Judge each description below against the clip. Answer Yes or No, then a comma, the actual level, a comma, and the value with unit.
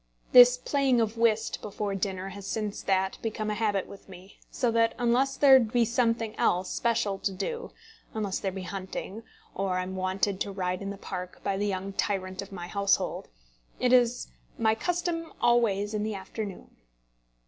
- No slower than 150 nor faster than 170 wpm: No, average, 180 wpm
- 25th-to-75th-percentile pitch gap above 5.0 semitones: No, average, 3.4 semitones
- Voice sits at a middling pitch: No, high, 205 Hz